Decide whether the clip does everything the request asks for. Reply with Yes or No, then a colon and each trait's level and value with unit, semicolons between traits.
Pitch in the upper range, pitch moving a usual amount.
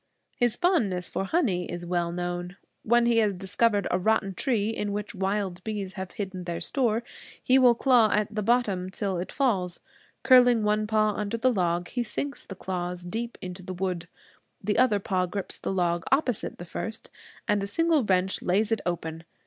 Yes: high, 200 Hz; average, 4.1 semitones